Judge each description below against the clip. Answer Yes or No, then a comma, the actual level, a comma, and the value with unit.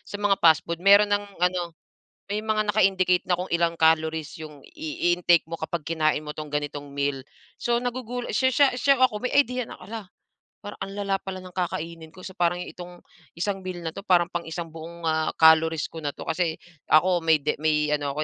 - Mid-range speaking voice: Yes, medium, 175 Hz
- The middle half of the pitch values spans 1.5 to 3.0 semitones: No, average, 3.7 semitones